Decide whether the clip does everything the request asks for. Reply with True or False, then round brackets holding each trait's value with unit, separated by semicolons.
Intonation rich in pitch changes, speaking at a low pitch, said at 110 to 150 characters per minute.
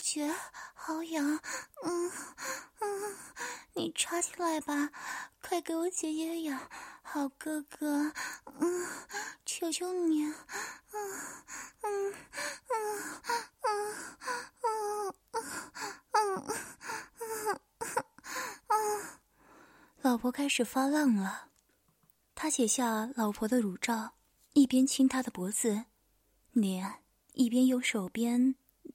False (8.0 semitones; 315 Hz; 125 characters per minute)